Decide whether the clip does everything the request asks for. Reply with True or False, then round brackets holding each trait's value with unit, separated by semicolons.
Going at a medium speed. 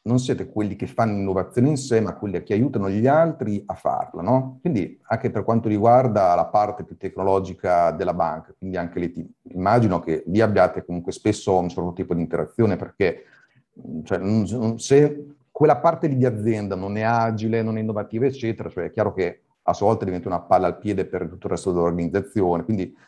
False (195 wpm)